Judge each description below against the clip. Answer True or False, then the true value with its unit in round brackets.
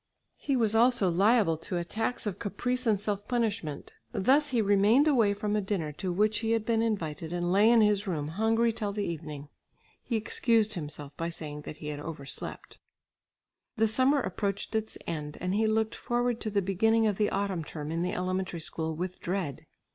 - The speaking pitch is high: True (205 Hz)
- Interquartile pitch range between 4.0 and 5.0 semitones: True (4.7 semitones)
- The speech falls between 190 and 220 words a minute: True (195 wpm)